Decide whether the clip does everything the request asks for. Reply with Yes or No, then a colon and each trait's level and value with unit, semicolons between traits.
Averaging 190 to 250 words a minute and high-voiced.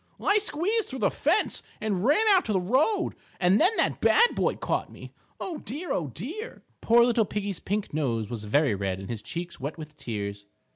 Yes: average, 200 wpm; high, 195 Hz